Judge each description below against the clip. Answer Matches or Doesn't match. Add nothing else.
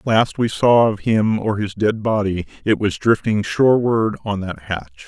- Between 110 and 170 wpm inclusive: Doesn't match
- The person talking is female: Doesn't match